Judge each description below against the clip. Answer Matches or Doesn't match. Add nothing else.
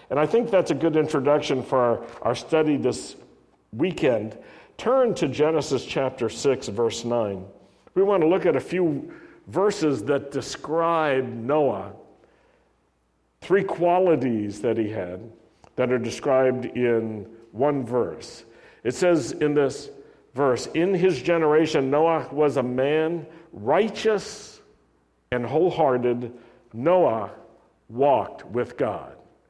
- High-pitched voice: Doesn't match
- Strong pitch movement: Matches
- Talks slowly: Matches